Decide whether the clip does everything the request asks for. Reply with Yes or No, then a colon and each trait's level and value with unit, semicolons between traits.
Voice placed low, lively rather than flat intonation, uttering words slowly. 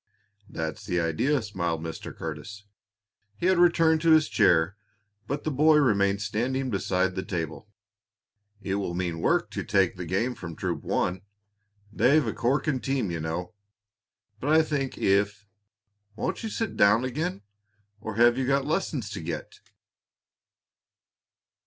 No: low, 105 Hz; wide, 7.3 semitones; average, 145 wpm